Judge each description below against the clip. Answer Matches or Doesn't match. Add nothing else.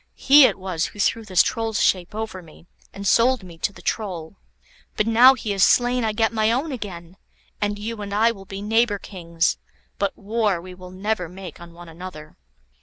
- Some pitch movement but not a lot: Matches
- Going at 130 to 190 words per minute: Doesn't match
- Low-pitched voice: Doesn't match